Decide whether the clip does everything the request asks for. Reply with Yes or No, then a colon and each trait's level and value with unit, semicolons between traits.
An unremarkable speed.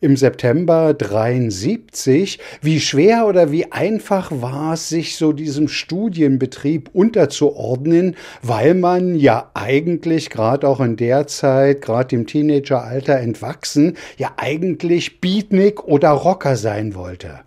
No: slow, 120 wpm